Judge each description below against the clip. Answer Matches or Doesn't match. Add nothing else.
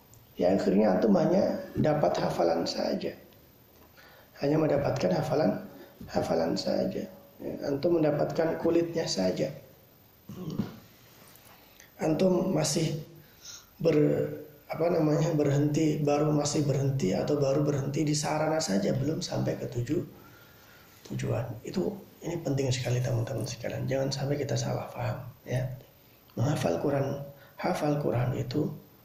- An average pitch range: Matches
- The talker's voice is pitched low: Doesn't match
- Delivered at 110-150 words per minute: Matches